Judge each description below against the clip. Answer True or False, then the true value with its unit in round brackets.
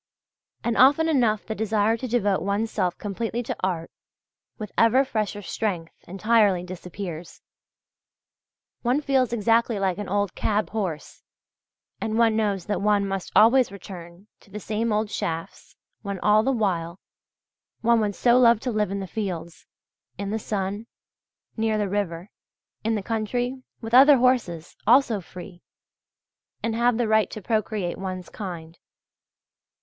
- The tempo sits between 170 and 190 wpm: False (150 wpm)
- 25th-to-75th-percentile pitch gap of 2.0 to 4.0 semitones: True (3.2 semitones)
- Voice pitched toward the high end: True (210 Hz)